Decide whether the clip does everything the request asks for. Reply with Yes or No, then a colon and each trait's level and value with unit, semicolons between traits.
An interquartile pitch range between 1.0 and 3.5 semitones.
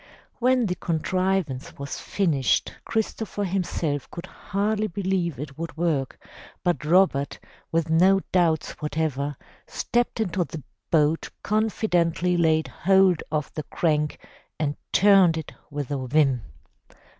No: average, 4.2 semitones